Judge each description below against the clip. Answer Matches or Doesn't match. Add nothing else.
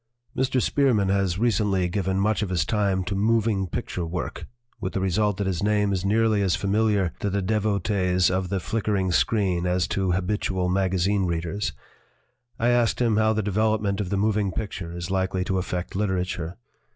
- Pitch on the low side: Matches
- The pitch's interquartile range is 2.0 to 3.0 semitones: Matches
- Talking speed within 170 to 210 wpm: Matches